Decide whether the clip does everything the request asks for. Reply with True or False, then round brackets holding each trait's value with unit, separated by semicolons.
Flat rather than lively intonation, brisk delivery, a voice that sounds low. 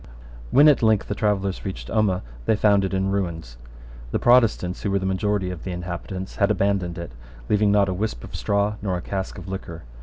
True (2.2 semitones; 210 wpm; 95 Hz)